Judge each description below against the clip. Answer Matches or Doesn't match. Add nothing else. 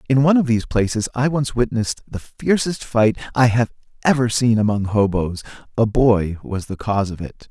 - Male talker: Matches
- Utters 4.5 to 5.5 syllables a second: Matches